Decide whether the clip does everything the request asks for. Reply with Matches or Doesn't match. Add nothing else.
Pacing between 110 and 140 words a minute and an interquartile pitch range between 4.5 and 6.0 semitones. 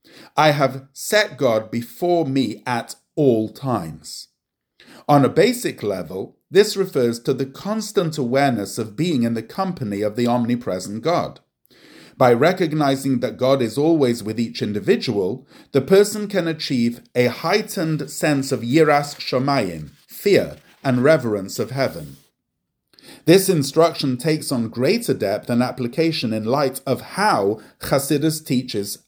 Matches